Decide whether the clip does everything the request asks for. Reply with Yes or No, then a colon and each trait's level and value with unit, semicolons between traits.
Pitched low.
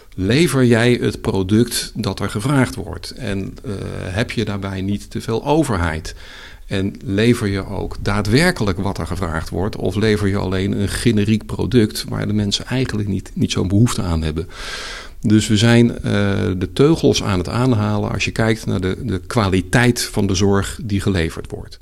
Yes: low, 105 Hz